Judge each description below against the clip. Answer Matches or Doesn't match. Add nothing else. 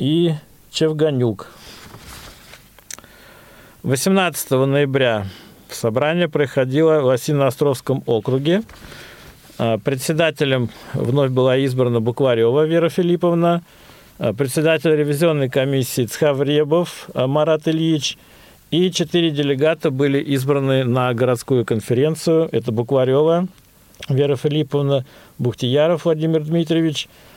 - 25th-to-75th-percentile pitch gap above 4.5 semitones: Doesn't match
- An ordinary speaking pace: Doesn't match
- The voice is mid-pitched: Matches